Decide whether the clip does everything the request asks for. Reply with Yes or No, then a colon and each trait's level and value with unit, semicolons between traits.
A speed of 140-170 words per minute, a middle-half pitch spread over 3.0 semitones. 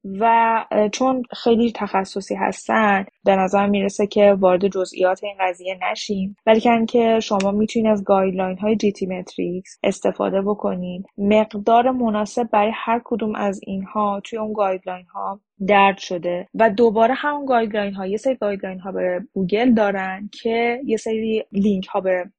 No: average, 145 wpm; average, 2.7 semitones